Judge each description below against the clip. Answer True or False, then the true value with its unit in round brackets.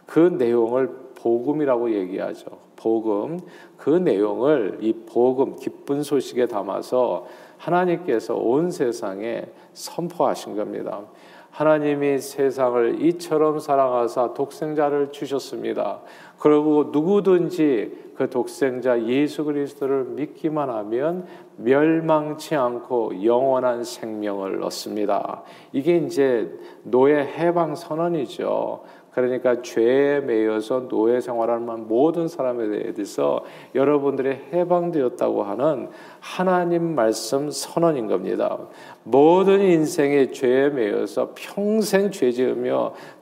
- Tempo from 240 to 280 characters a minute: True (255 characters per minute)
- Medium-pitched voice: True (145 Hz)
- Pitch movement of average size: True (4.9 semitones)